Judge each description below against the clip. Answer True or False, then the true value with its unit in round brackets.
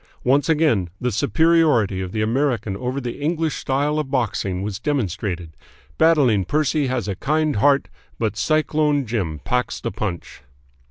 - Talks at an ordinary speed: True (150 wpm)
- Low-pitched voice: True (125 Hz)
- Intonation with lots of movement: True (6.3 semitones)